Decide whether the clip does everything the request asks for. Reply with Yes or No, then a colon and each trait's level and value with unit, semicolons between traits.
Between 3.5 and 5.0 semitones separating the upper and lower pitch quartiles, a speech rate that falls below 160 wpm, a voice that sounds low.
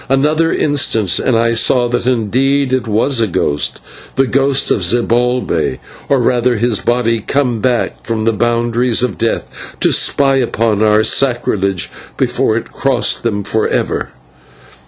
No: average, 2.8 semitones; average, 145 wpm; low, 120 Hz